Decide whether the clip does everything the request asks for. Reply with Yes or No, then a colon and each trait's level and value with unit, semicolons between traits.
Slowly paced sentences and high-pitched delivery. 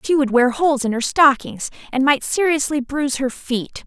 No: average, 200 wpm; very high, 275 Hz